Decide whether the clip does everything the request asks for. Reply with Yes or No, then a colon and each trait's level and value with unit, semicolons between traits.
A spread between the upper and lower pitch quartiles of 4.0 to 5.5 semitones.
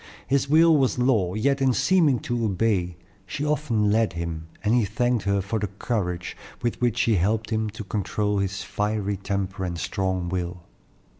Yes: average, 4.3 semitones